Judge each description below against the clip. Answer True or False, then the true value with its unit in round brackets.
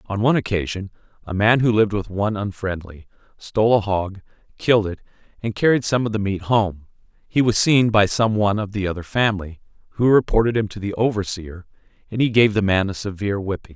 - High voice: False (105 Hz)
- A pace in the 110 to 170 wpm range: False (200 wpm)